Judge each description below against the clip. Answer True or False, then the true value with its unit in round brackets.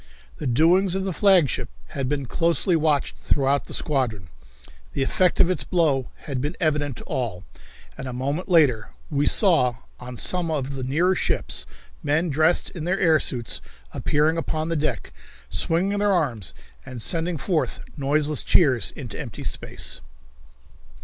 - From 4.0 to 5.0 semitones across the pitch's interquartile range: True (4.3 semitones)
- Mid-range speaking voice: True (150 Hz)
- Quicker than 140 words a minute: True (155 wpm)